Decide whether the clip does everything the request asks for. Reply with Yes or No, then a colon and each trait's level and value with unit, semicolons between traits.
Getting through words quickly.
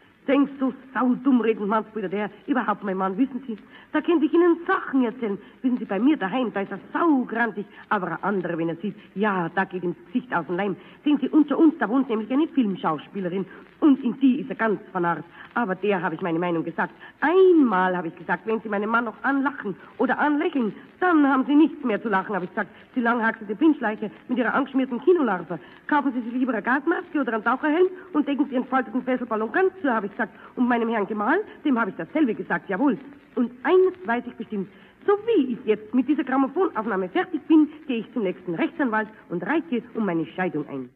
Yes: fast, 215 wpm